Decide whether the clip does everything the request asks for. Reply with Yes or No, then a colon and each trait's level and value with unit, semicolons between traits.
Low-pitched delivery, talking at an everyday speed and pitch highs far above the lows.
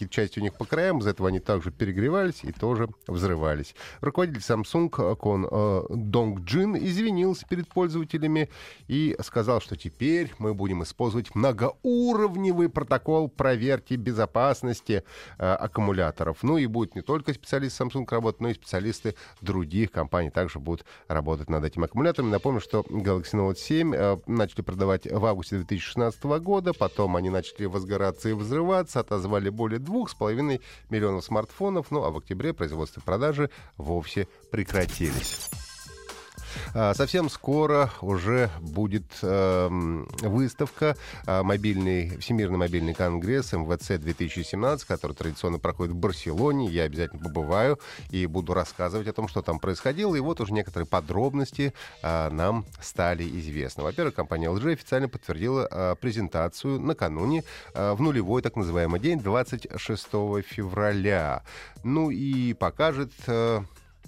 Yes: low, 105 Hz; average, 135 wpm; wide, 6.5 semitones